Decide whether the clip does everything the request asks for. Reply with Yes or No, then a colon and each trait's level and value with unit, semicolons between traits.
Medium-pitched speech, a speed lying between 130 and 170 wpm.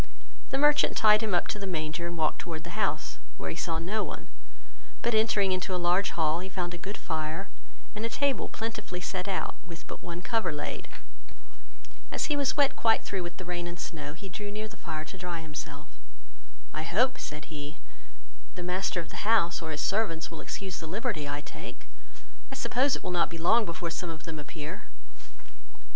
No: medium, 180 Hz; fast, 205 wpm